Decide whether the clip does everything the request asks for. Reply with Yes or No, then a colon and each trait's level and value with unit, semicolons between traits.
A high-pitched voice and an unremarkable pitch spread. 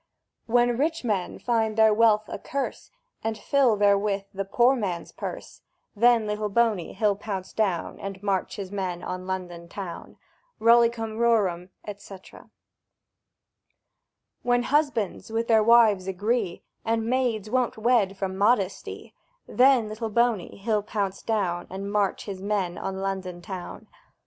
Yes: high, 210 Hz; average, 3.2 semitones